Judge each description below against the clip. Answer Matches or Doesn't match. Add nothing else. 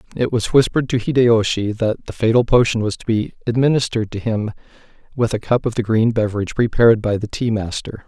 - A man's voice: Matches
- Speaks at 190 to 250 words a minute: Matches